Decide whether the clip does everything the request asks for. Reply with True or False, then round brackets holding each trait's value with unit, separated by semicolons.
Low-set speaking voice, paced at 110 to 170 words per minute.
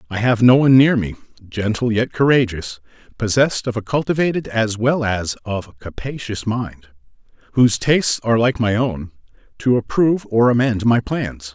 True (115 Hz; 165 wpm)